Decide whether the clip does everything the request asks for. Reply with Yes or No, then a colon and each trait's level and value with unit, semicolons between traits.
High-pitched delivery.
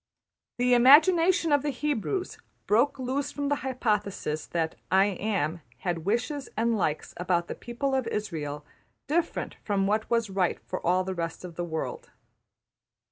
Yes: high, 220 Hz